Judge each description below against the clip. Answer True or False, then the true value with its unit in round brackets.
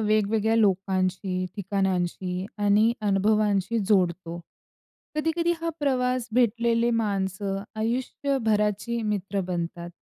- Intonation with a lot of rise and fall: False (3.3 semitones)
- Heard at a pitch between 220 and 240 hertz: False (210 Hz)